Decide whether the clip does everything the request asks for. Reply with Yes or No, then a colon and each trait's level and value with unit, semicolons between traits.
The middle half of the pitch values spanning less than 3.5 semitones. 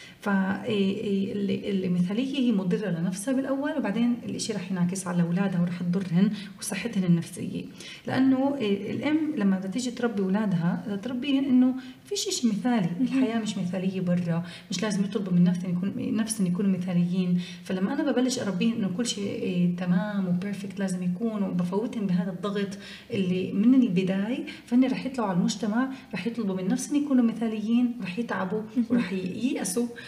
No: average, 4.2 semitones